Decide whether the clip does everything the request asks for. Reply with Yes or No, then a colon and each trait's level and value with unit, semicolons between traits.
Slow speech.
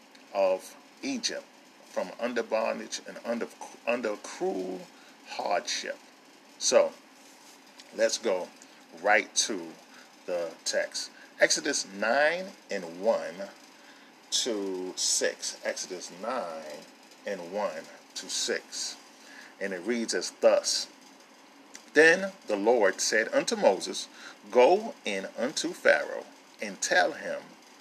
Yes: slow, 100 wpm